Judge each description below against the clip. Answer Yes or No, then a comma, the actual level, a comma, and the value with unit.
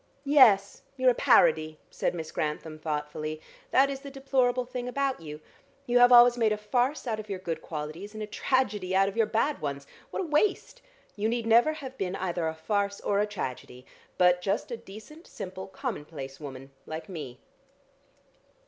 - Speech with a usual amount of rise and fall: No, wide, 7.5 semitones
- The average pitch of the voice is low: No, high, 205 Hz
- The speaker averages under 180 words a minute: No, average, 185 wpm